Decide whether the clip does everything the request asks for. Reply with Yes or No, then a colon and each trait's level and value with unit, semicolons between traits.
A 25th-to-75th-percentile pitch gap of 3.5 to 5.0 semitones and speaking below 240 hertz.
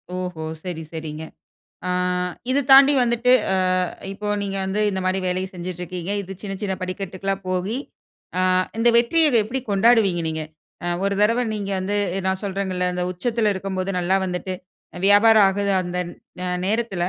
No: average, 2.7 semitones; high, 190 Hz